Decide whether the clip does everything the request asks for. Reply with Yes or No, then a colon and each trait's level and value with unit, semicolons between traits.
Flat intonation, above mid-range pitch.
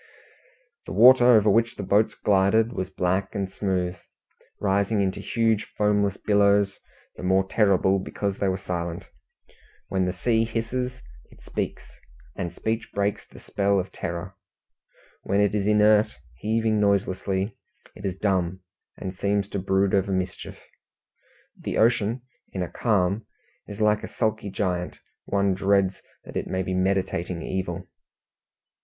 No: narrow, 2.2 semitones; low, 100 Hz